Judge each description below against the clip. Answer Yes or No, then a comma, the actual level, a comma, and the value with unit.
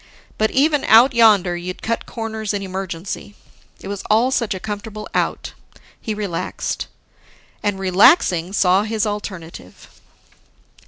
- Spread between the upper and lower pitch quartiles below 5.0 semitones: Yes, average, 2.9 semitones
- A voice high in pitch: Yes, high, 205 Hz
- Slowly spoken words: Yes, slow, 125 wpm